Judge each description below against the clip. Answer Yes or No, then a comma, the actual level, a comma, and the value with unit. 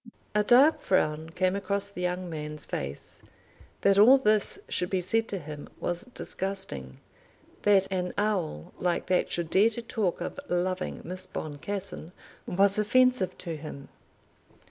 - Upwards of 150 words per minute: No, average, 145 wpm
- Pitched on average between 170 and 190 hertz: Yes, medium, 185 Hz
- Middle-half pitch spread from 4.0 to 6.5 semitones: No, average, 3.3 semitones